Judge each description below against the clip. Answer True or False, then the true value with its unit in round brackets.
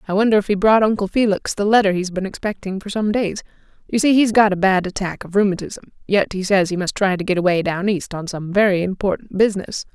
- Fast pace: True (240 wpm)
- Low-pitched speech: False (195 Hz)